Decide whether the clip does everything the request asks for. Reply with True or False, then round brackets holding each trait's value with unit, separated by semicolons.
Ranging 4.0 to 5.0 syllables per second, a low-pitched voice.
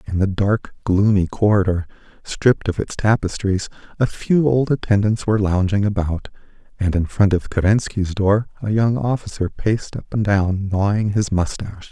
True (4.9 syllables/s; 100 Hz)